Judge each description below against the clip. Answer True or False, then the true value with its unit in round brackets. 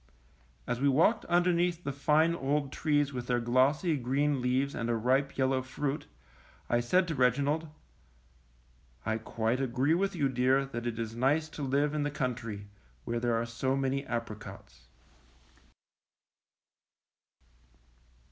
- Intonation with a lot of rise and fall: False (3.3 semitones)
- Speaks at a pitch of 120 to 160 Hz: True (135 Hz)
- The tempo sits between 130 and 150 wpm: True (140 wpm)